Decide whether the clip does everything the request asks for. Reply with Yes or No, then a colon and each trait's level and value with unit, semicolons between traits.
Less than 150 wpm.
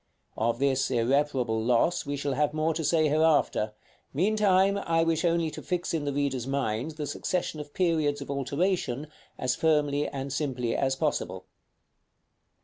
No: average, 155 wpm